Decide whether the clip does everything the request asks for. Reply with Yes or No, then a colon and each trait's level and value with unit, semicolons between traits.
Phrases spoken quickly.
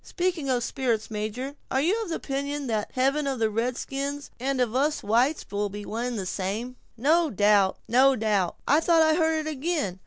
Yes: fast, 210 wpm